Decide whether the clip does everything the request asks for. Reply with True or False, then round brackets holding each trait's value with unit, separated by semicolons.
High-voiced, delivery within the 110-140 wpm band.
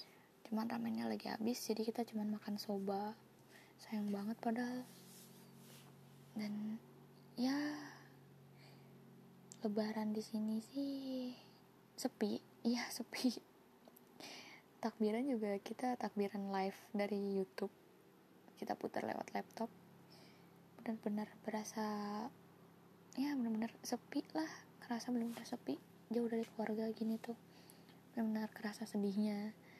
False (215 Hz; 100 wpm)